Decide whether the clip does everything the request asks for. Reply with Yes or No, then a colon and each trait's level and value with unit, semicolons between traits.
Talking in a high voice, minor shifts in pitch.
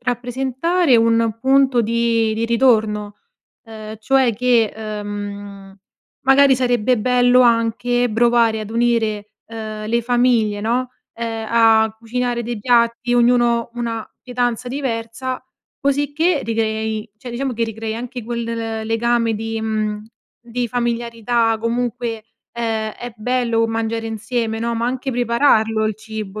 Yes: high, 230 Hz; narrow, 1.9 semitones